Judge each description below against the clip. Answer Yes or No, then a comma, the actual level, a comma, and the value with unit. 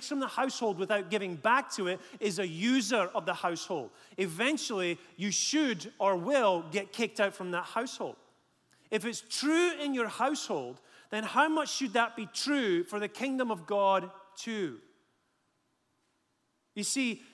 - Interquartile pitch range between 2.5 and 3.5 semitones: No, average, 5.3 semitones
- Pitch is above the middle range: Yes, high, 220 Hz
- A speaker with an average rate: Yes, average, 160 wpm